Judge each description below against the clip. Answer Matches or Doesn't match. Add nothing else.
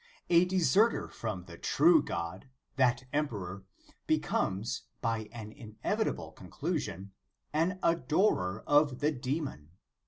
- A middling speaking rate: Doesn't match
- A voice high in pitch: Doesn't match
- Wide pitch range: Matches